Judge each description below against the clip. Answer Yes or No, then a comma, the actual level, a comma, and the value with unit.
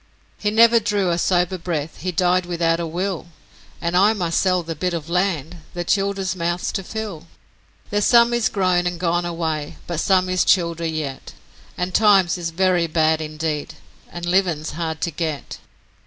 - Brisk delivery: No, average, 175 wpm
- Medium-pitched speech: Yes, medium, 175 Hz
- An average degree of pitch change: No, narrow, 2.3 semitones